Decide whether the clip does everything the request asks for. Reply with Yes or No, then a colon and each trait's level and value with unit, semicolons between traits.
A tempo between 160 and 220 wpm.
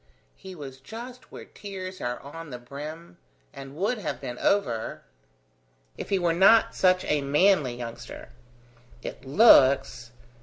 No: average, 140 wpm